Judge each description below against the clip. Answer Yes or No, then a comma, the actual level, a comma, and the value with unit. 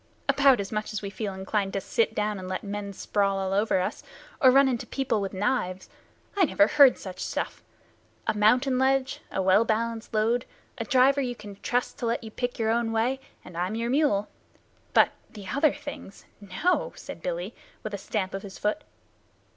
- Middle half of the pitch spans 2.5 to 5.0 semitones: Yes, average, 4.4 semitones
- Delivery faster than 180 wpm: Yes, average, 195 wpm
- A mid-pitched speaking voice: No, high, 220 Hz